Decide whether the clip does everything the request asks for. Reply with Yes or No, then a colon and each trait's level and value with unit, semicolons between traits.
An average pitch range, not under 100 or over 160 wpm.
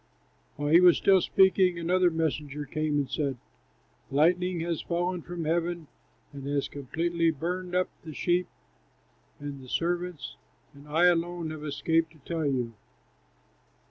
Yes: average, 3.2 semitones; average, 140 wpm